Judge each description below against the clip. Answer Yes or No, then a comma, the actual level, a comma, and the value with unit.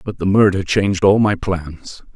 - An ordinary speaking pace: Yes, average, 195 wpm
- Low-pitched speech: Yes, very low, 95 Hz